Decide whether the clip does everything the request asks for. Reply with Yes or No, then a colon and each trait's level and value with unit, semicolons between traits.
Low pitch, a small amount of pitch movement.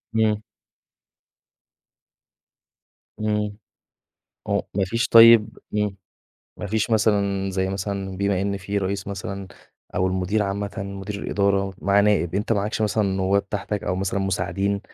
Yes: low, 100 Hz; narrow, 1.3 semitones